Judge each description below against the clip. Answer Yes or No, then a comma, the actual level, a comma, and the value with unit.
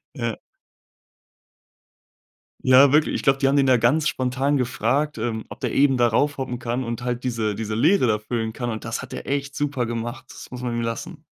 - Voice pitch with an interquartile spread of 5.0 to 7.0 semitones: No, average, 2.7 semitones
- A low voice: Yes, low, 125 Hz